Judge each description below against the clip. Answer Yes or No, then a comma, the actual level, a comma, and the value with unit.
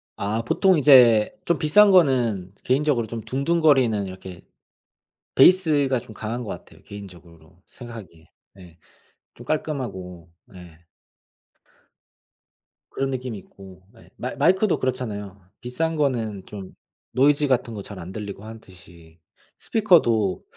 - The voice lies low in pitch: Yes, low, 115 Hz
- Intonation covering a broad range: Yes, wide, 6.4 semitones